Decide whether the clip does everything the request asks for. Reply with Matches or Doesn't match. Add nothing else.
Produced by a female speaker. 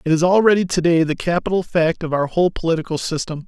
Doesn't match